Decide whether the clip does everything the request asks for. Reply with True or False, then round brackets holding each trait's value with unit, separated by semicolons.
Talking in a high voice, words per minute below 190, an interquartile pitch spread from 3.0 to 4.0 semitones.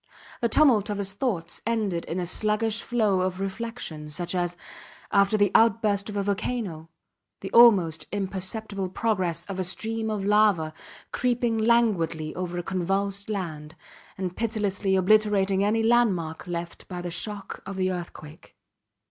True (195 Hz; 150 wpm; 3.5 semitones)